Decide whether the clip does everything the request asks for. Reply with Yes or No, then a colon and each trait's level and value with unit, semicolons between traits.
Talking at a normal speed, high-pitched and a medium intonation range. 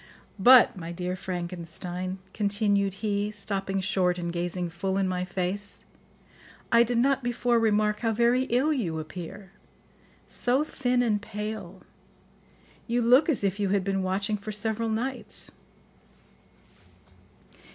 No: slow, 130 wpm; high, 205 Hz; average, 3.9 semitones